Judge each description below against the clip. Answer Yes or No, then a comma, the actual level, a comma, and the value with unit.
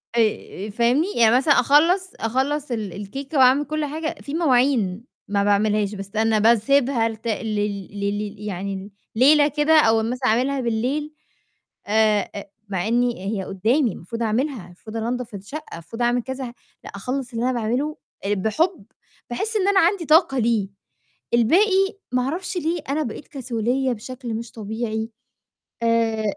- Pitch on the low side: No, high, 235 Hz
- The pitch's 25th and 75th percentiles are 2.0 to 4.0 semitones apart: No, average, 4.7 semitones